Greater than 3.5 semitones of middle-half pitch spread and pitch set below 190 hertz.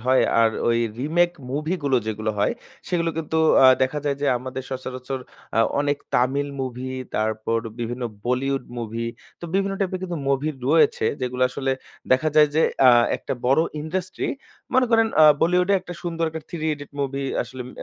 Yes: average, 4.5 semitones; medium, 140 Hz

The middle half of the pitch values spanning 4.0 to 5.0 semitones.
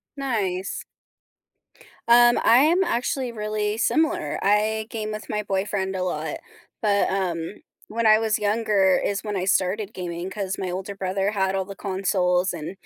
No: narrow, 2.5 semitones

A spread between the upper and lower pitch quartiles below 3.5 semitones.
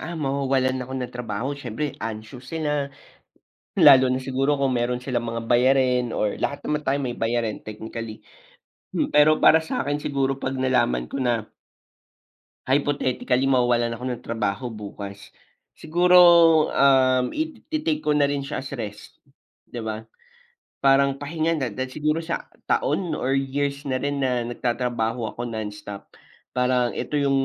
Yes: average, 2.9 semitones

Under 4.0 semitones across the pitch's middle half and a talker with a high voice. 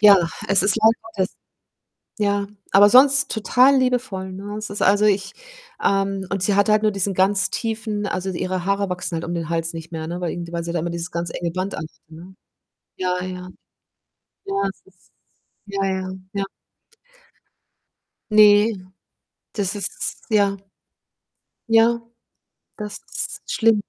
Yes: narrow, 2.6 semitones; high, 195 Hz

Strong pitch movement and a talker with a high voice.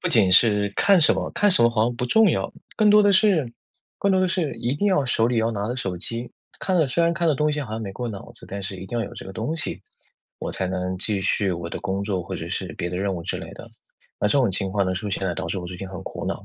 No: wide, 7.7 semitones; low, 110 Hz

